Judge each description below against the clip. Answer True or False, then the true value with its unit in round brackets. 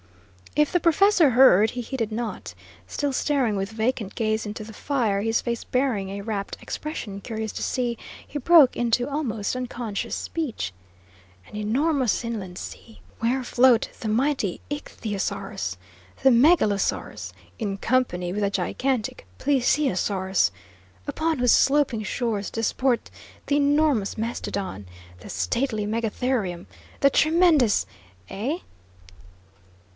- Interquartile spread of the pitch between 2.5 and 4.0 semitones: False (4.7 semitones)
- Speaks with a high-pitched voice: True (235 Hz)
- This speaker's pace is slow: True (120 wpm)